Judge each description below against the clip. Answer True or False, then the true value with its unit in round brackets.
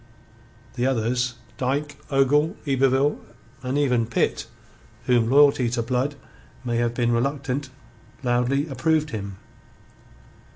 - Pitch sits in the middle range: False (130 Hz)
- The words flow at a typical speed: False (110 wpm)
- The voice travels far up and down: False (2.7 semitones)